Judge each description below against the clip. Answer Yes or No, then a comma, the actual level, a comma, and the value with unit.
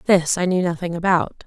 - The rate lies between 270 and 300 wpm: No, fast, 205 wpm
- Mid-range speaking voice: Yes, medium, 180 Hz